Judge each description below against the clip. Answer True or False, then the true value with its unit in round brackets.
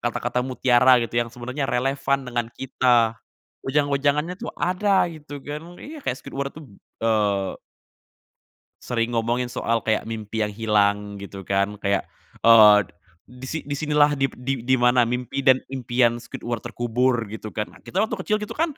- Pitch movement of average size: True (3.4 semitones)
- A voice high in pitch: False (125 Hz)